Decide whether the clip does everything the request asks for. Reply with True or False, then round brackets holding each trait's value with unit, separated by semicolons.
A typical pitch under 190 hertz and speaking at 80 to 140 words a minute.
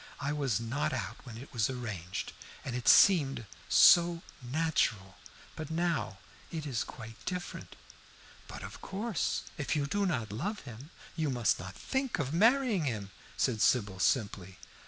False (135 Hz; 155 wpm)